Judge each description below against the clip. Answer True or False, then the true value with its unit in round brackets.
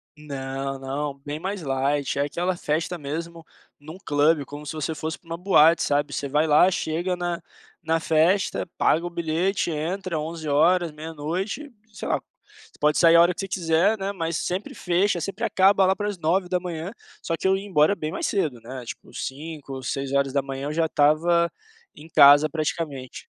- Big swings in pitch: False (3.4 semitones)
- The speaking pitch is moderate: True (160 Hz)